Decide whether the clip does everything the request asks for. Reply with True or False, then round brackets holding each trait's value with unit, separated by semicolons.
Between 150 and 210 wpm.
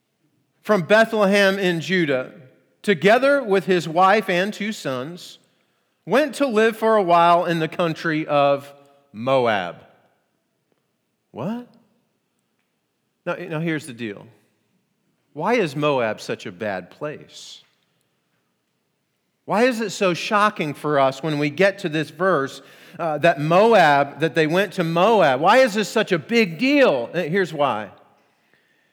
False (135 wpm)